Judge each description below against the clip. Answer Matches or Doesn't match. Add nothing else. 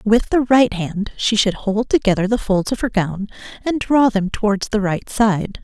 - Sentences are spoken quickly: Matches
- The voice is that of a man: Doesn't match